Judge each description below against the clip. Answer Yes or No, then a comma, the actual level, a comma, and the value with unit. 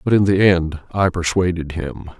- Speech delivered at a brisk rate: No, average, 190 wpm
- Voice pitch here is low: Yes, very low, 90 Hz